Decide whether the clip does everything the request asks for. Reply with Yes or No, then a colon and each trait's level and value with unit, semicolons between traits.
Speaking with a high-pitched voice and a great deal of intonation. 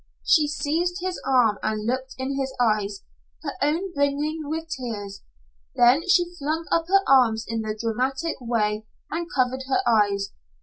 Yes: very high, 265 Hz; wide, 6.1 semitones